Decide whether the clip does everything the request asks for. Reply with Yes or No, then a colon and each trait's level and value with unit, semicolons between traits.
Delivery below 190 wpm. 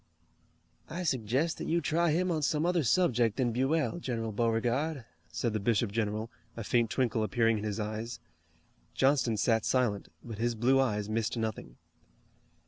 Yes: average, 160 wpm